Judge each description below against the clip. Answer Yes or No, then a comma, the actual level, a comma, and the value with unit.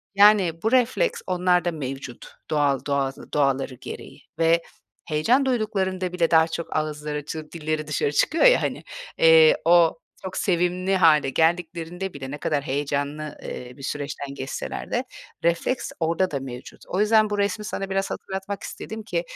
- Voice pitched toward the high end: No, medium, 165 Hz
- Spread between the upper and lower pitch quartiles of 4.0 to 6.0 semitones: Yes, average, 4.6 semitones